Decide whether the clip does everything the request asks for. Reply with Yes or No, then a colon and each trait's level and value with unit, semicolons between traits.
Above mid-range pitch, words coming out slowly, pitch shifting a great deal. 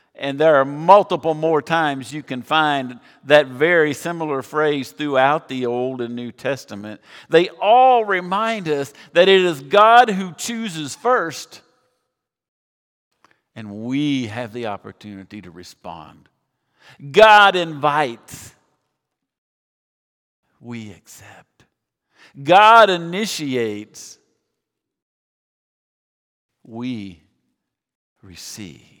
No: medium, 145 Hz; slow, 95 wpm; wide, 6.7 semitones